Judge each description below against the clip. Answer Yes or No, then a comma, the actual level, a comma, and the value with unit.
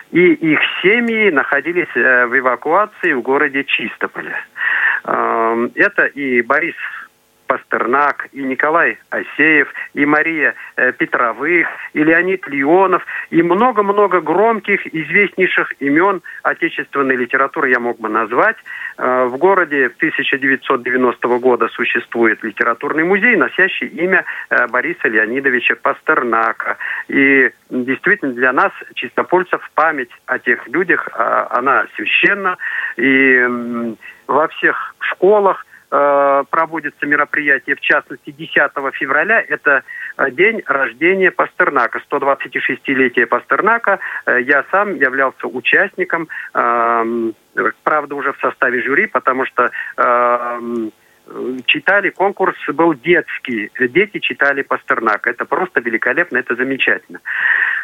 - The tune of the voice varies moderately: No, wide, 5.9 semitones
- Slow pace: Yes, slow, 100 wpm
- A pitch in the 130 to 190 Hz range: Yes, medium, 140 Hz